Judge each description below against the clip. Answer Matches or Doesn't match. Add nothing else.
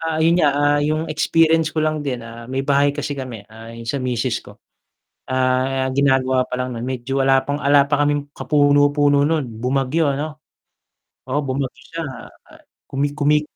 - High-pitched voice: Doesn't match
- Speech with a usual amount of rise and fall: Doesn't match